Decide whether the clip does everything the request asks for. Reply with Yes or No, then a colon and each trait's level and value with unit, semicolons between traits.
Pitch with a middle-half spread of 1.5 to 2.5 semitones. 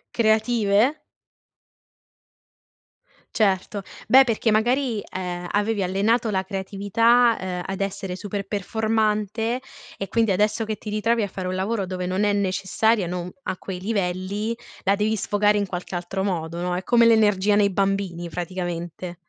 No: average, 2.9 semitones